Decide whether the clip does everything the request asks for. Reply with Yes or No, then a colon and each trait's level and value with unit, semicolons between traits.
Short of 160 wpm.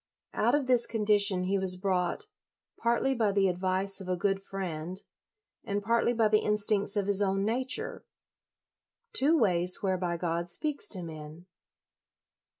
Yes: average, 150 wpm